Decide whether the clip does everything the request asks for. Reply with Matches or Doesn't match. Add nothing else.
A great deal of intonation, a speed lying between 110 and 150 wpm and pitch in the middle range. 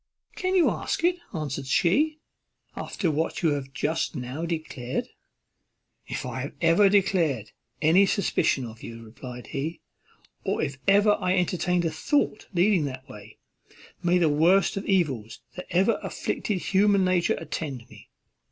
Matches